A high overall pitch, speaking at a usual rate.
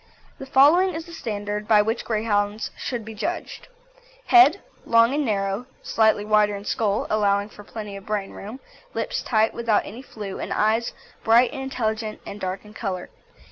Yes: high, 215 Hz; average, 175 wpm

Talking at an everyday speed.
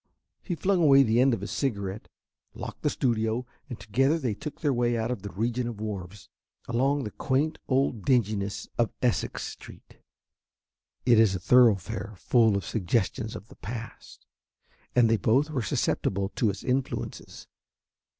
Yes: average, 160 wpm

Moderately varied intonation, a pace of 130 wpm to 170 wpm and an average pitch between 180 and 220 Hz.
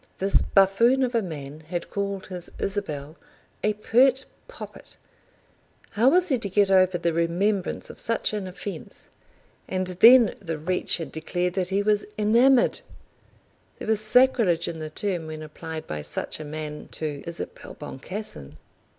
Yes: average, 4.7 semitones; average, 155 wpm; high, 190 Hz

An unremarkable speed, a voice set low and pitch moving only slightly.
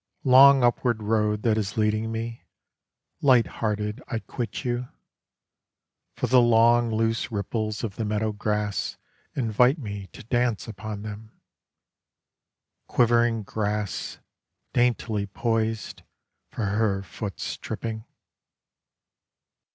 No: slow, 105 wpm; low, 110 Hz; narrow, 2.0 semitones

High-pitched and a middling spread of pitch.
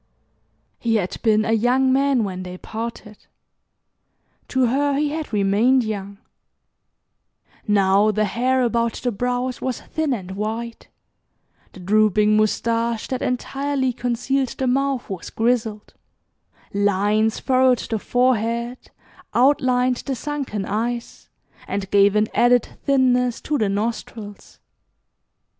Yes: high, 235 Hz; average, 3.3 semitones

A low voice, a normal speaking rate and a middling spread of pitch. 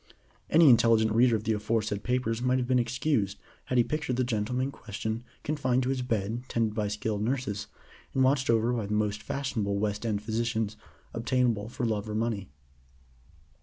Yes: low, 115 Hz; average, 180 wpm; average, 3.0 semitones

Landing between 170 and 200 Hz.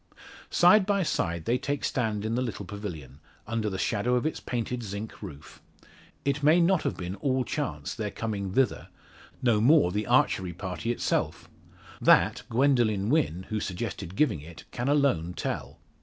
No: low, 110 Hz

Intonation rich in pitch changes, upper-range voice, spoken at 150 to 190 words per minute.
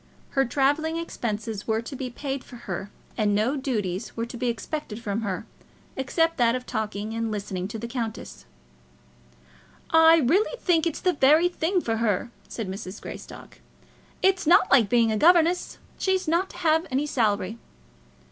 Yes: wide, 6.8 semitones; high, 245 Hz; average, 165 wpm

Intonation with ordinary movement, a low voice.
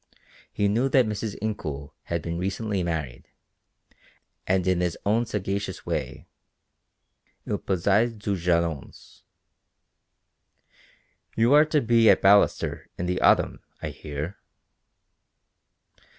Yes: average, 4.3 semitones; very low, 95 Hz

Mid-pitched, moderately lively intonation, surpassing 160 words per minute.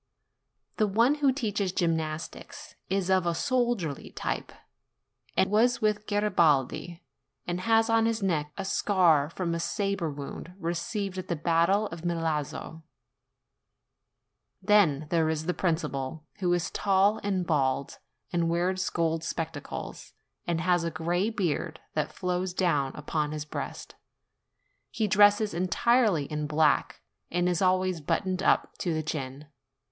No: medium, 175 Hz; average, 3.9 semitones; average, 140 wpm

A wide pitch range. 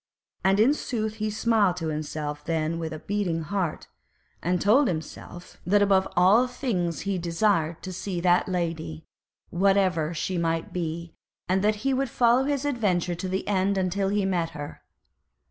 No: average, 3.7 semitones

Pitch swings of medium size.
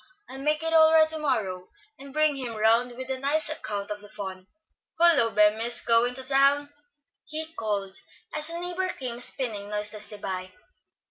No: wide, 6.4 semitones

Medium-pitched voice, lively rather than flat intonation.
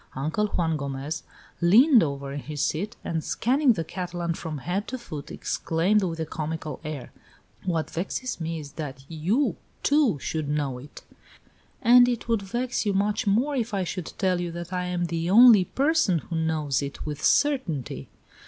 Yes: medium, 175 Hz; wide, 5.7 semitones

